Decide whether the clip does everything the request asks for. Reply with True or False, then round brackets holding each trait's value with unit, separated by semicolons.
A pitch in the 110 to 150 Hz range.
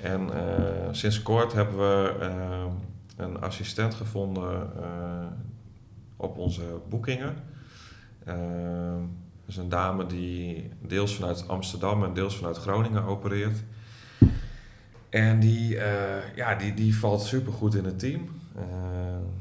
False (100 Hz)